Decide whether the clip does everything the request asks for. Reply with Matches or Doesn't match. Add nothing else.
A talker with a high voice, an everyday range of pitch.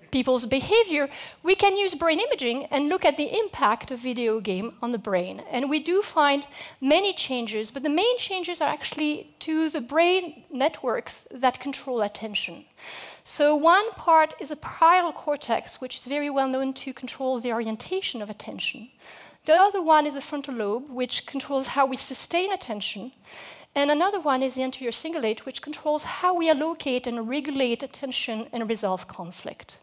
Matches